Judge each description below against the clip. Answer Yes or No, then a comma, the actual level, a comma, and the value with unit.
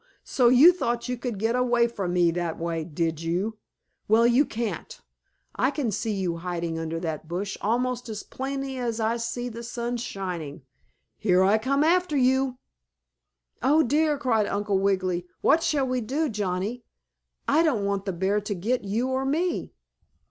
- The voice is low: No, high, 225 Hz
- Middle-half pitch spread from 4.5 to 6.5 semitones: Yes, average, 5.3 semitones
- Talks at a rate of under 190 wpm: Yes, average, 175 wpm